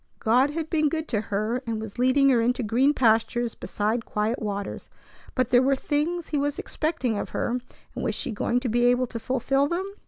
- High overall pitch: Yes, very high, 250 Hz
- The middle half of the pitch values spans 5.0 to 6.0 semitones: No, average, 4.0 semitones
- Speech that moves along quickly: Yes, fast, 210 wpm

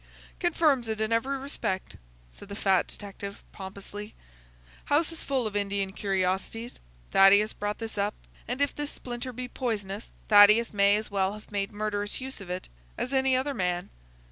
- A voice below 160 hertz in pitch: No, high, 210 Hz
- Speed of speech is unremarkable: Yes, average, 170 wpm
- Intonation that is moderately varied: Yes, average, 4.1 semitones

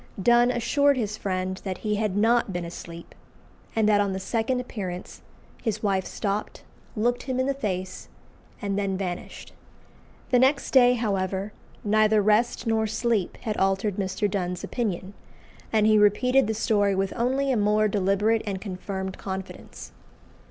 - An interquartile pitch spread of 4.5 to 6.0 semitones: No, average, 3.2 semitones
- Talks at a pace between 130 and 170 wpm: Yes, average, 155 wpm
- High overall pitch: Yes, high, 210 Hz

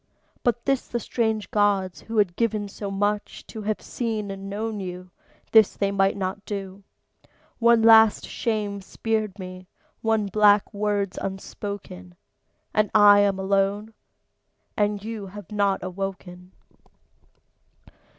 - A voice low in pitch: No, high, 205 Hz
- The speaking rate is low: Yes, slow, 125 wpm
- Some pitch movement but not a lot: No, narrow, 1.9 semitones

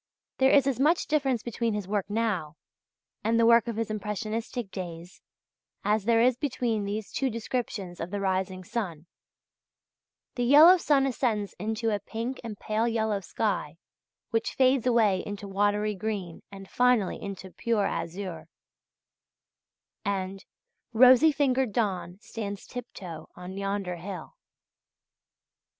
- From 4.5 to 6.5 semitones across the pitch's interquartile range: No, average, 3.6 semitones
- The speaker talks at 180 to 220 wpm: No, average, 145 wpm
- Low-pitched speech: No, high, 215 Hz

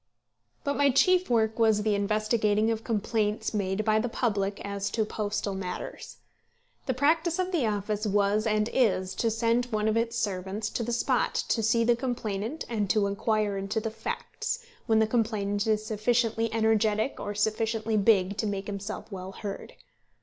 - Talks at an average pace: Yes, average, 170 wpm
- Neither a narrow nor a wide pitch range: No, narrow, 2.1 semitones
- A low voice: No, high, 215 Hz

